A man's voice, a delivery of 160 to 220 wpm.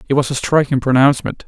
Yes: male; fast, 205 wpm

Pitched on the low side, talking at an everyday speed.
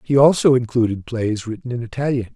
Yes: low, 120 Hz; average, 180 wpm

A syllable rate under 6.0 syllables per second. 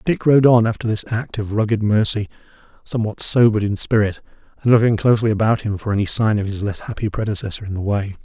No: 6.4 syllables/s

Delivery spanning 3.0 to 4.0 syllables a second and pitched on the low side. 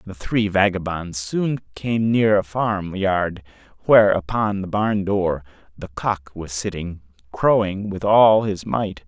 Yes: 3.8 syllables/s; low, 100 Hz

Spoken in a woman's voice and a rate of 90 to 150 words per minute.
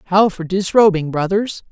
Yes: female; average, 140 wpm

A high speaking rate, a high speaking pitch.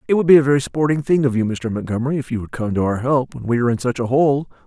No: fast, 320 wpm; low, 130 Hz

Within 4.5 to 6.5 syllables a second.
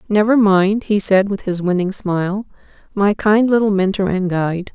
Yes: 4.8 syllables/s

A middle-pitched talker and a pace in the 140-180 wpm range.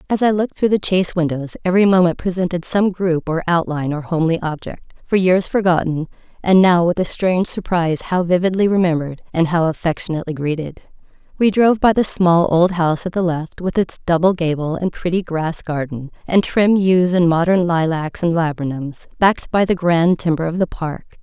No: medium, 175 Hz; average, 190 wpm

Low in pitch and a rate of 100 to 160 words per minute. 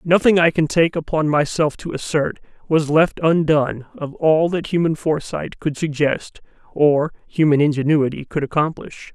No: medium, 155 Hz; average, 150 wpm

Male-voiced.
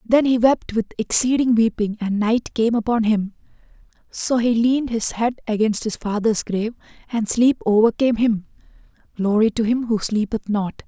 No: female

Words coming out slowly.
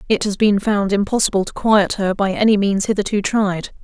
No: fast, 205 wpm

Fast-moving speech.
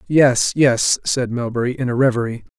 No: average, 165 wpm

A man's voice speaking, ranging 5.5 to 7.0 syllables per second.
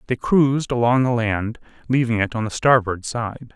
No: male; 4.9 syllables/s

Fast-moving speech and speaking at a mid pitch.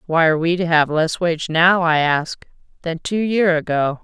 Yes: fast, 210 wpm; medium, 165 Hz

